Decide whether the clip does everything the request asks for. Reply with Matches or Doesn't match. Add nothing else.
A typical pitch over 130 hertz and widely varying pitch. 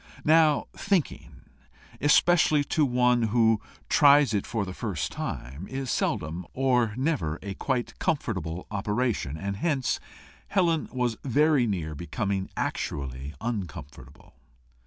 Doesn't match